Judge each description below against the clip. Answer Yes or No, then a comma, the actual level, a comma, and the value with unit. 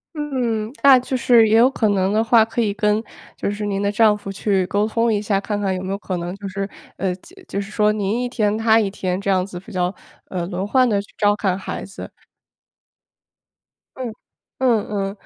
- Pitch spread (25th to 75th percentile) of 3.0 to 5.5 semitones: No, narrow, 2.4 semitones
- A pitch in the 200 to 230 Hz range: Yes, high, 205 Hz